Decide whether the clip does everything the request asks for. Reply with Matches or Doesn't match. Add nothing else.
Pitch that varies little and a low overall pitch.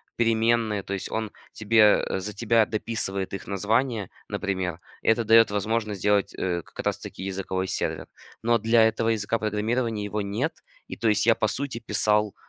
Matches